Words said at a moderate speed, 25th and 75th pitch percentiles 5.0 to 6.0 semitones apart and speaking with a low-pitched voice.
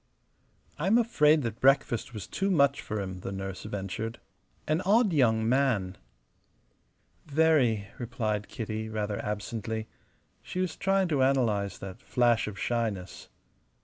No: slow, 130 wpm; wide, 5.5 semitones; low, 115 Hz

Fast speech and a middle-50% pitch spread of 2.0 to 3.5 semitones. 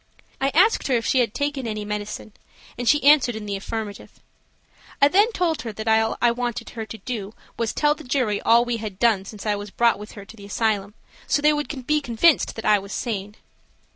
No: fast, 225 wpm; average, 4.5 semitones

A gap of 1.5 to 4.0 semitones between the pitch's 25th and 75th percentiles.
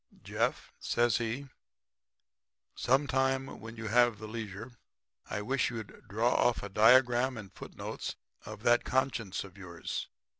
Yes: average, 3.1 semitones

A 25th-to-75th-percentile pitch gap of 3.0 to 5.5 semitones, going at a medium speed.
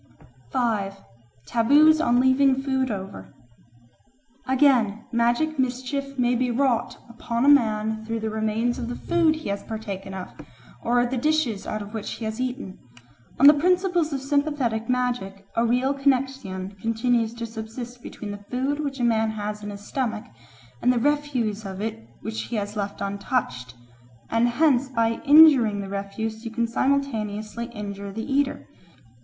Yes: average, 3.9 semitones; average, 160 wpm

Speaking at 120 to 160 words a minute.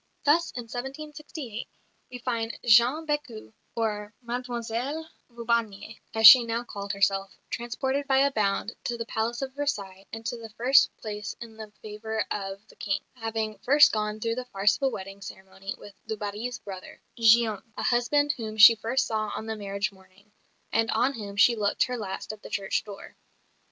No: average, 180 wpm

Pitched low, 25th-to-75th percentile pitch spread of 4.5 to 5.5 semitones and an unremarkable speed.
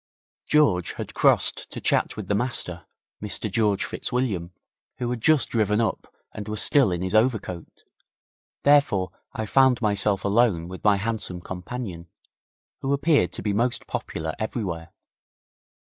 Yes: low, 105 Hz; average, 4.9 semitones; average, 145 wpm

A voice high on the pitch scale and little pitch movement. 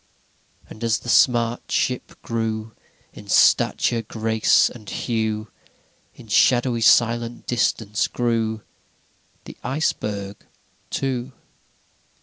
No: low, 115 Hz; narrow, 1.6 semitones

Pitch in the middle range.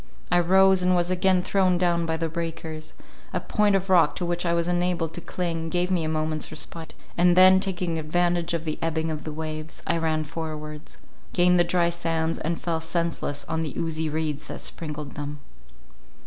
Yes: medium, 165 Hz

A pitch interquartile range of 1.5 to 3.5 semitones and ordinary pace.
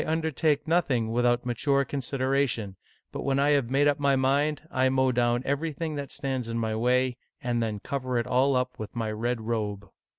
Yes: average, 2.9 semitones; average, 190 wpm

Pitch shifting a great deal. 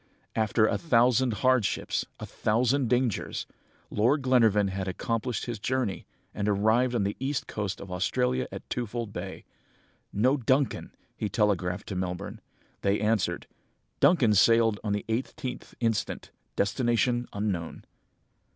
No: average, 3.7 semitones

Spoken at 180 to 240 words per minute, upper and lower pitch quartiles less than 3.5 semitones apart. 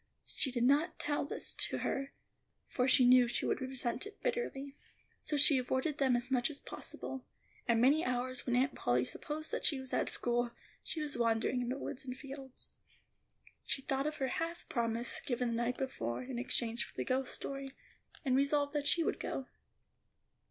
Yes: average, 190 wpm; narrow, 2.5 semitones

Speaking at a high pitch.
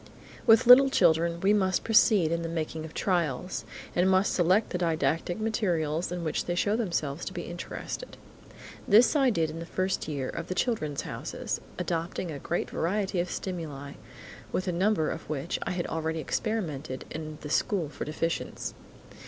No: medium, 175 Hz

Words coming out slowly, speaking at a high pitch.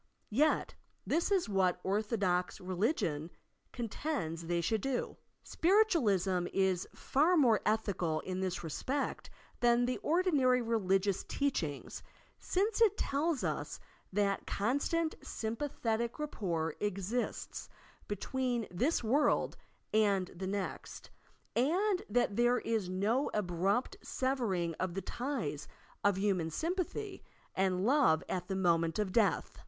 Yes: slow, 125 wpm; high, 215 Hz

